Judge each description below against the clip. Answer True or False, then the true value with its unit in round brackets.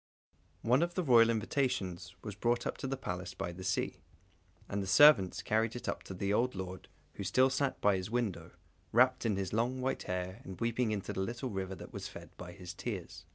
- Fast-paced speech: True (210 wpm)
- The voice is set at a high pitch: False (105 Hz)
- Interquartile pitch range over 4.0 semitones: True (4.7 semitones)